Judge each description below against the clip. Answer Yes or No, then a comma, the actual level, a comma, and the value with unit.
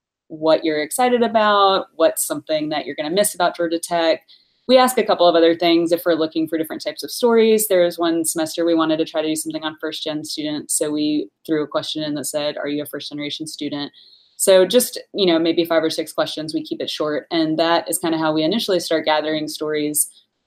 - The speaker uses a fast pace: Yes, fast, 240 wpm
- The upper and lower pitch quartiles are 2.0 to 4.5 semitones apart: No, average, 5.2 semitones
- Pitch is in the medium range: Yes, medium, 165 Hz